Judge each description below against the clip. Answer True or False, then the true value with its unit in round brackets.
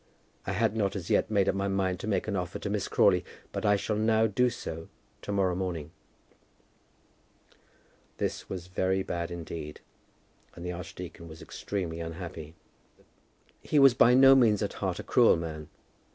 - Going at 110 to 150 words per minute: False (170 wpm)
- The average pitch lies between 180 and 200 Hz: False (95 Hz)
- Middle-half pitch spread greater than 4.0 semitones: False (3.5 semitones)